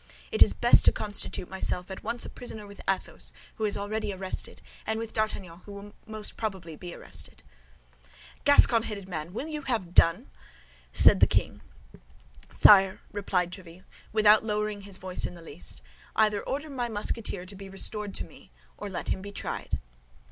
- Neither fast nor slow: Yes, average, 170 wpm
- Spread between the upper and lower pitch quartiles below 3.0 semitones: Yes, narrow, 2.5 semitones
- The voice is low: No, high, 205 Hz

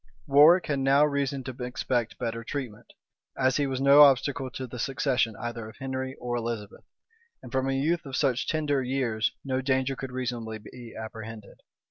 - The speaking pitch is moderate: No, low, 130 Hz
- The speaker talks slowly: No, average, 175 wpm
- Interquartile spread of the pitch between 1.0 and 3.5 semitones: Yes, narrow, 2.6 semitones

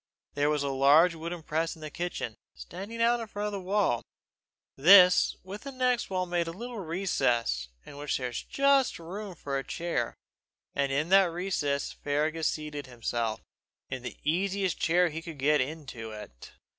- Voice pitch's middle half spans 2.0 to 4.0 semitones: No, wide, 5.4 semitones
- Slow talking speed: No, average, 170 wpm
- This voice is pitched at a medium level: Yes, medium, 165 Hz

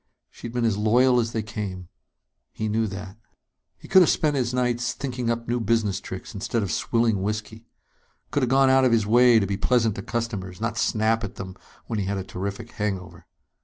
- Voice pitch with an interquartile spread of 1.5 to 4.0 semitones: Yes, average, 2.9 semitones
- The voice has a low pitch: Yes, low, 115 Hz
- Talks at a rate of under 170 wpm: No, fast, 205 wpm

